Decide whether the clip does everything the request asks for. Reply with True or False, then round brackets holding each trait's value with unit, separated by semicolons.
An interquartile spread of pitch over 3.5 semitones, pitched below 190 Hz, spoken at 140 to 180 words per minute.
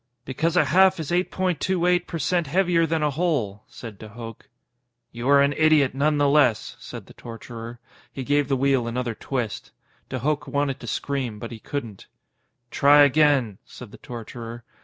False (4.4 semitones; 140 Hz; 190 wpm)